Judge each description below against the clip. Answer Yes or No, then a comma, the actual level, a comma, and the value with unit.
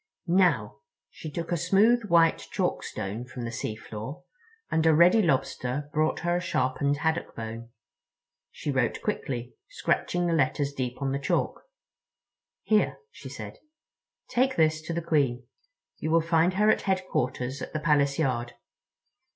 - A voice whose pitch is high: No, medium, 155 Hz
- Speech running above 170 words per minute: No, average, 145 wpm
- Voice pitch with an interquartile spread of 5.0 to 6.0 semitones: Yes, average, 5.3 semitones